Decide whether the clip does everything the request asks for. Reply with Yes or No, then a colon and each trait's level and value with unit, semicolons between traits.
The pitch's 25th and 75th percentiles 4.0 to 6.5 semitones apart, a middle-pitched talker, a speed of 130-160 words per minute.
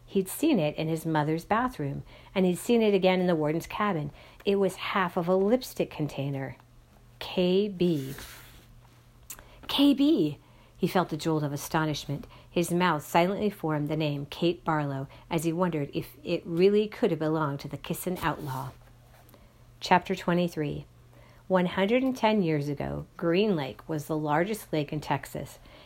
Yes: average, 4.6 semitones; medium, 160 Hz; average, 150 wpm